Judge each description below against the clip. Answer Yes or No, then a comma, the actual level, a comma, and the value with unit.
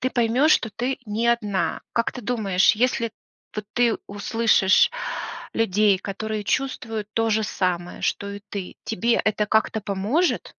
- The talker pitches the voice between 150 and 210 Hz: No, high, 220 Hz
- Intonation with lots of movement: No, average, 2.7 semitones